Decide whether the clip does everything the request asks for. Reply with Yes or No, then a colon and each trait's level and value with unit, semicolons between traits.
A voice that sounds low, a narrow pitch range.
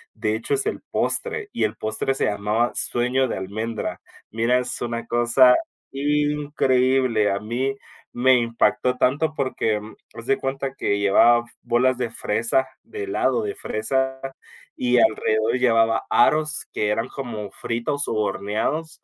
No: low, 120 Hz; average, 3.2 semitones